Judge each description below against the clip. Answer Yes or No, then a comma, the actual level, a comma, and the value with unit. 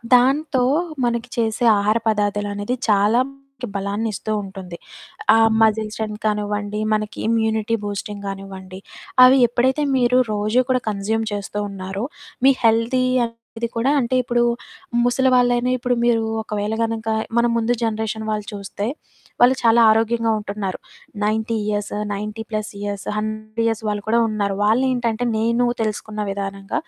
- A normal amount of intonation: No, narrow, 2.3 semitones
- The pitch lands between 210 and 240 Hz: Yes, high, 220 Hz